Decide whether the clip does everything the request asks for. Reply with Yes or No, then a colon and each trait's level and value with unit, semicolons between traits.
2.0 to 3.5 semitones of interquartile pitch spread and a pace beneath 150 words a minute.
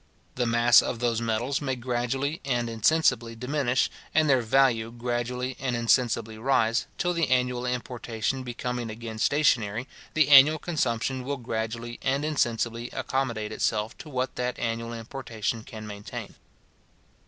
Yes: narrow, 2.5 semitones; average, 140 wpm